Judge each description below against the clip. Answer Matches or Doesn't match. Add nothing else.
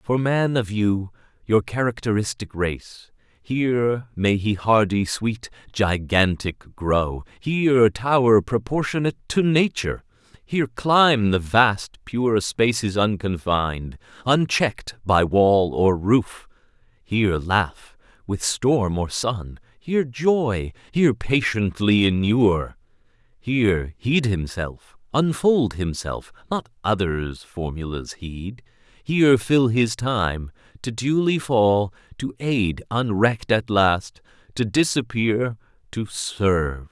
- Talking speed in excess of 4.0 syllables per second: Doesn't match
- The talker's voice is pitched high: Doesn't match